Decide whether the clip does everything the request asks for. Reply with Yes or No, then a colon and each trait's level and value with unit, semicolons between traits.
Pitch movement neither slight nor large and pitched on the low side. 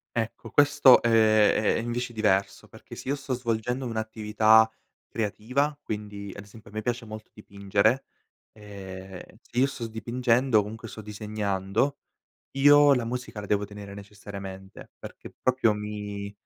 Yes: average, 3.0 semitones; low, 110 Hz